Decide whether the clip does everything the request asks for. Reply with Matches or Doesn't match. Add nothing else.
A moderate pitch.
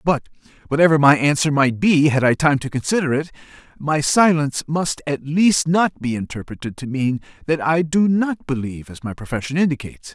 Matches